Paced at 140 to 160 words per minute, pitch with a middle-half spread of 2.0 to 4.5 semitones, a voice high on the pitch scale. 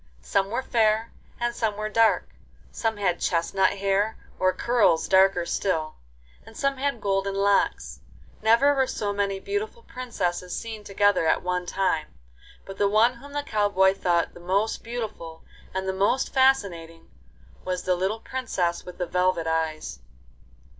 Yes: average, 155 wpm; average, 3.9 semitones; high, 200 Hz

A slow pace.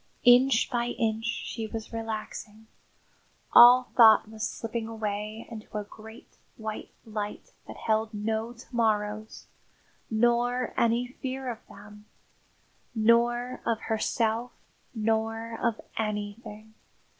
Yes: slow, 110 wpm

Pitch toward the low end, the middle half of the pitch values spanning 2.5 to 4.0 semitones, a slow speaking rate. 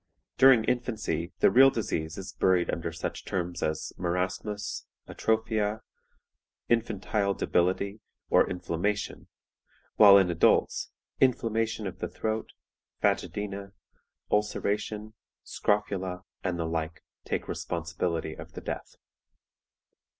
Yes: low, 100 Hz; average, 3.7 semitones; slow, 105 wpm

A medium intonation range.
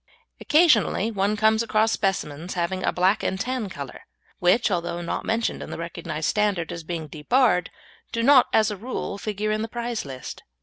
Yes: average, 4.6 semitones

